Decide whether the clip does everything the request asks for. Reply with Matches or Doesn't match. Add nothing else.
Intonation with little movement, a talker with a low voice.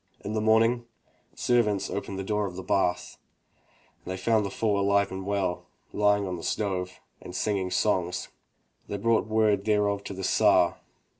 Matches